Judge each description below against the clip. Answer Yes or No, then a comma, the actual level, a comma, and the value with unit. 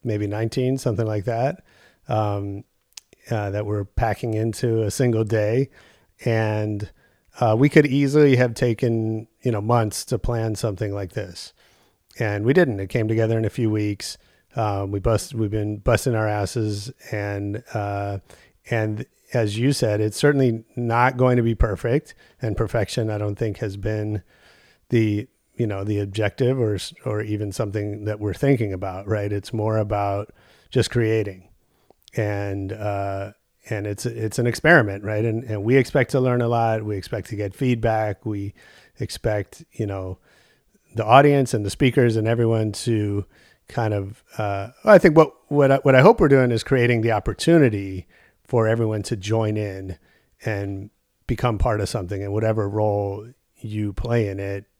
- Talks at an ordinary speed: Yes, average, 170 wpm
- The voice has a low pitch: Yes, low, 110 Hz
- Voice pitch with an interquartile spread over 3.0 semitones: No, average, 2.7 semitones